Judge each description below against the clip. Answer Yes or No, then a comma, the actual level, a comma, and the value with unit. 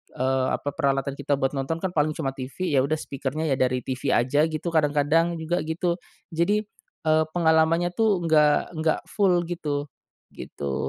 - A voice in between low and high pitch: Yes, medium, 155 Hz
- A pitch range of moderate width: Yes, average, 3.5 semitones